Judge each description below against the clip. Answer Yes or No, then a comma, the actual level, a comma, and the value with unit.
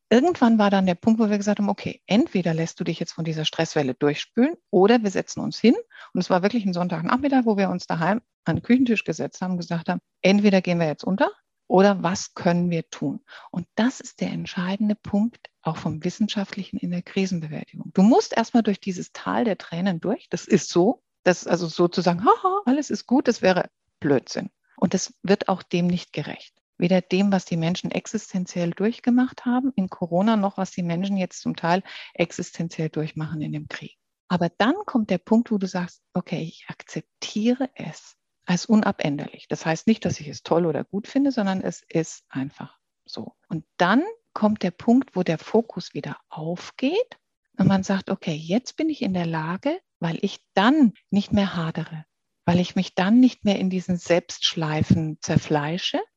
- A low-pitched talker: No, high, 190 Hz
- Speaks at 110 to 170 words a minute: No, fast, 190 wpm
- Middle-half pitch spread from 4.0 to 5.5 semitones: Yes, average, 4.4 semitones